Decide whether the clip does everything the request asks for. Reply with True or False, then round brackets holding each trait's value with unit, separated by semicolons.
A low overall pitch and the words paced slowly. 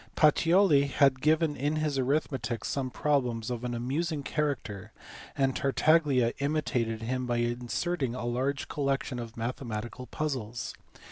True (130 Hz; 130 wpm)